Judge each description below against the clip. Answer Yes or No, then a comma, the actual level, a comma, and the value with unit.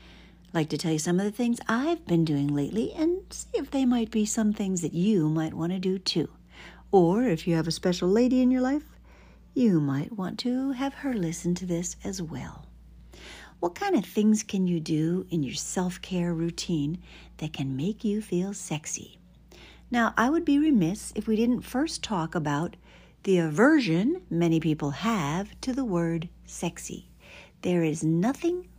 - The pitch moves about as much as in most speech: No, wide, 6.7 semitones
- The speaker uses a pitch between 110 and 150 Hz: No, medium, 185 Hz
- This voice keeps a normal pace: Yes, average, 185 wpm